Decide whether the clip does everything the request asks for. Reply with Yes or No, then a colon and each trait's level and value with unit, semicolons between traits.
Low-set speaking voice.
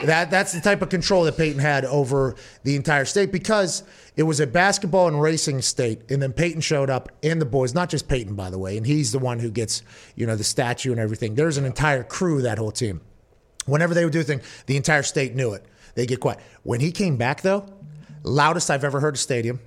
No: medium, 145 Hz